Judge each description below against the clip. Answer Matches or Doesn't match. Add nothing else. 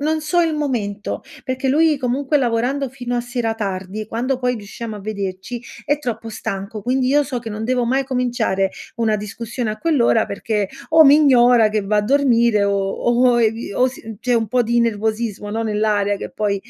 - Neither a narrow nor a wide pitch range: Matches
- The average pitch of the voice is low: Doesn't match